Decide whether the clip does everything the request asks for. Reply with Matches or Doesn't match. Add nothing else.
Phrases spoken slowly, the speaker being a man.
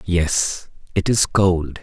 Matches